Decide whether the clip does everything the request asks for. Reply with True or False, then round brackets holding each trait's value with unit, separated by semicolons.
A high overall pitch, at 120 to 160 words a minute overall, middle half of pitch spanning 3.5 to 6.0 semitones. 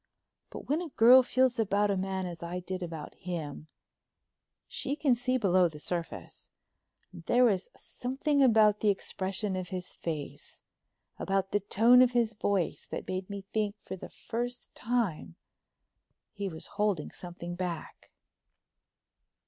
True (200 Hz; 150 wpm; 5.0 semitones)